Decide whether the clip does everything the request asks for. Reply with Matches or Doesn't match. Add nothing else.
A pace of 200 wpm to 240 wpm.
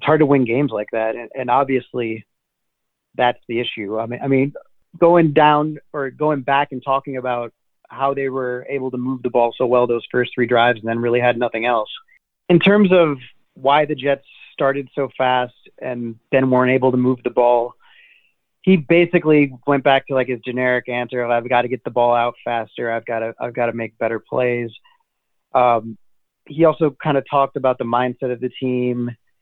Matches